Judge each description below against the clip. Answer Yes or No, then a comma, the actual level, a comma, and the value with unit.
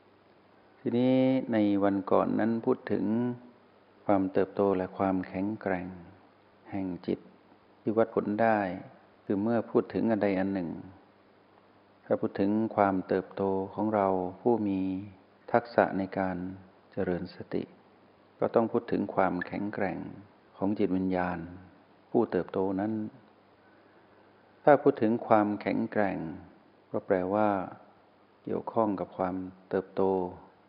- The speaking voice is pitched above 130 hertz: No, low, 100 Hz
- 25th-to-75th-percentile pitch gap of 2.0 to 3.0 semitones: Yes, narrow, 2.5 semitones